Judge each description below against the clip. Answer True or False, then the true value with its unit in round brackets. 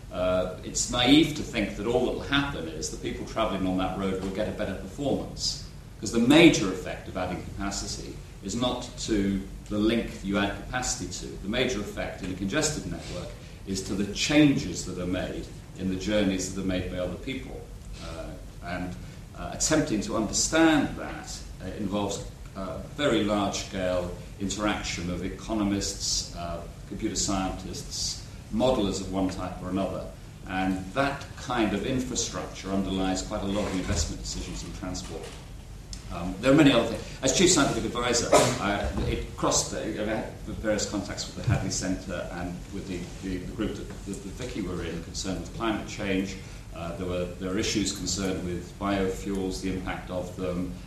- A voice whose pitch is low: True (95 Hz)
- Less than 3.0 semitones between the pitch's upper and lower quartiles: True (2.4 semitones)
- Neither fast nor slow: True (175 wpm)